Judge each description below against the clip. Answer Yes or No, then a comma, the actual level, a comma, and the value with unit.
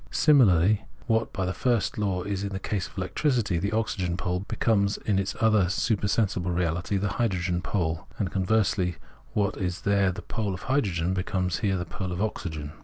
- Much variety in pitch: No, average, 2.8 semitones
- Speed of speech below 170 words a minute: No, average, 180 wpm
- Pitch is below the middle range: Yes, very low, 95 Hz